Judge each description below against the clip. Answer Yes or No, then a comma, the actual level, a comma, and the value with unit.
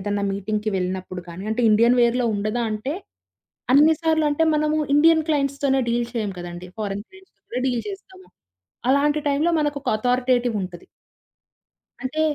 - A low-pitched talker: No, very high, 250 Hz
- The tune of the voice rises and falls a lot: Yes, wide, 5.9 semitones